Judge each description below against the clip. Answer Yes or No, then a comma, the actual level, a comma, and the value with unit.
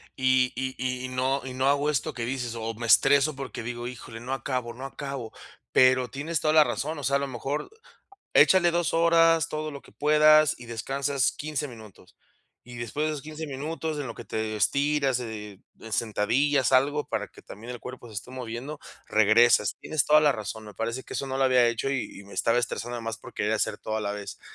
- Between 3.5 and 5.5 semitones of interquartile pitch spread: Yes, average, 3.9 semitones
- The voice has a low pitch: Yes, low, 130 Hz